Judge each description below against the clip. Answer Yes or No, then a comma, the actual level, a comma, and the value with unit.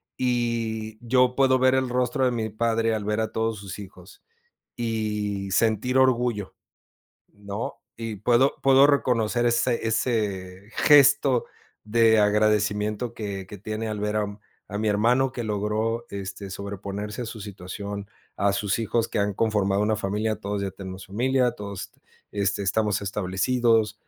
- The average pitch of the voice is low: Yes, low, 110 Hz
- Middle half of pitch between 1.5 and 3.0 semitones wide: Yes, narrow, 2.6 semitones